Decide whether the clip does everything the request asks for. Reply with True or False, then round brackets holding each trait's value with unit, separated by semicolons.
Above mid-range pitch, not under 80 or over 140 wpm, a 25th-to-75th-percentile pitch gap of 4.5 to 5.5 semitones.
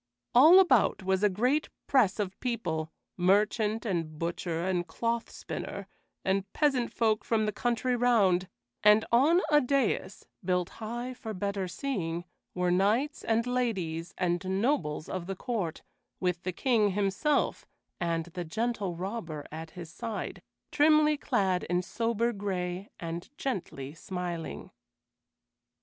True (200 Hz; 135 wpm; 5.0 semitones)